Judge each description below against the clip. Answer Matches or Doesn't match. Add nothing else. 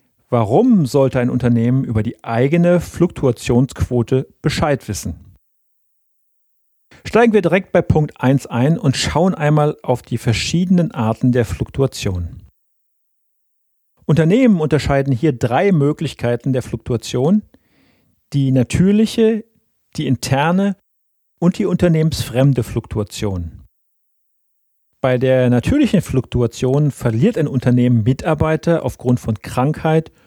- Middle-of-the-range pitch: Doesn't match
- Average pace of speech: Doesn't match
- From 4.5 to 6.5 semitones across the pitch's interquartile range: Matches